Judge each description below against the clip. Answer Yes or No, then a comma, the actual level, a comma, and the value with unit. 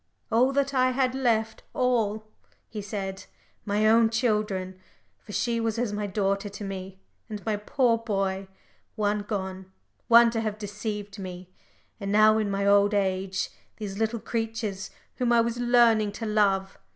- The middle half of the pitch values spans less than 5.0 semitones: Yes, narrow, 2.6 semitones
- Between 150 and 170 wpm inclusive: Yes, average, 160 wpm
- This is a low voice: No, high, 210 Hz